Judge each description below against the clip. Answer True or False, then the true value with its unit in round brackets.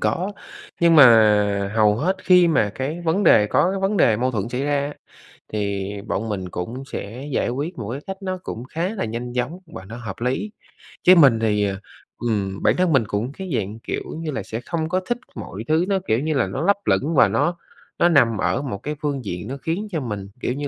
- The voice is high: False (130 Hz)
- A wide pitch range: True (7.6 semitones)